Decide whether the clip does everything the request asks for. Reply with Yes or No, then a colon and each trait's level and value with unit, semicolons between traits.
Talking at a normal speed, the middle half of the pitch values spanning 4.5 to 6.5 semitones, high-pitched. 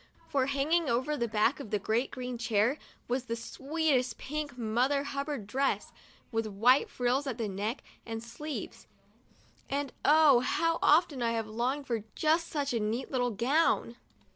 No: average, 165 wpm; average, 3.8 semitones; very high, 255 Hz